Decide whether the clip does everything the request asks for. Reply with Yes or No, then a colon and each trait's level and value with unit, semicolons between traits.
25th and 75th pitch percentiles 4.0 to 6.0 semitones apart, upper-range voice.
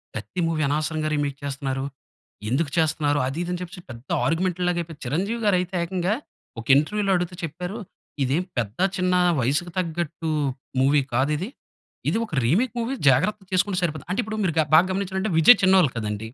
No: average, 4.5 semitones; medium, 165 Hz